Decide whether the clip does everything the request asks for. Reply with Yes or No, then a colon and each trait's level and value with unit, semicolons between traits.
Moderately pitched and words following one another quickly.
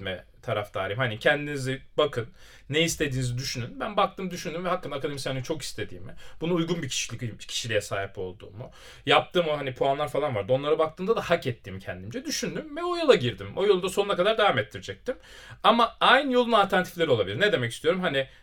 Yes: medium, 145 Hz; fast, 180 wpm